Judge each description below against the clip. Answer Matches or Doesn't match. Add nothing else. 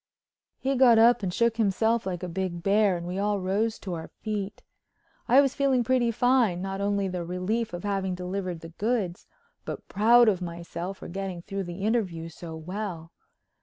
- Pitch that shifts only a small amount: Doesn't match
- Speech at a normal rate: Matches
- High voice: Matches